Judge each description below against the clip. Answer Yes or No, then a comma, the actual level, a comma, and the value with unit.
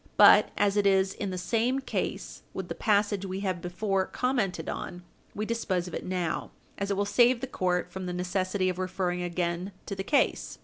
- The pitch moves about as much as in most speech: No, narrow, 2.3 semitones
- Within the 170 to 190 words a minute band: No, fast, 205 wpm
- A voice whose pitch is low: No, high, 190 Hz